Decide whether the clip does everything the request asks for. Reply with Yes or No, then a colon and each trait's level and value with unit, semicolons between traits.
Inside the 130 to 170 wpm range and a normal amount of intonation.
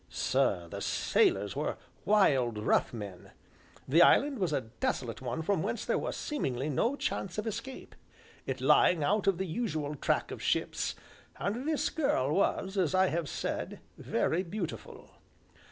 No: average, 155 wpm; wide, 7.8 semitones